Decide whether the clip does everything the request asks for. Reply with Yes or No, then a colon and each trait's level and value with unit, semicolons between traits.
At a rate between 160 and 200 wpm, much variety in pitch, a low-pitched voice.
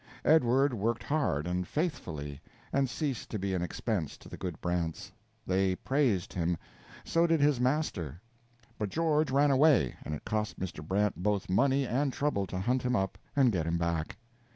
Yes: average, 175 wpm; wide, 7.7 semitones; low, 105 Hz